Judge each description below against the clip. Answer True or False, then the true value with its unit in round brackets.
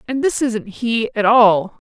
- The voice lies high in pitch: True (235 Hz)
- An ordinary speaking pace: True (195 wpm)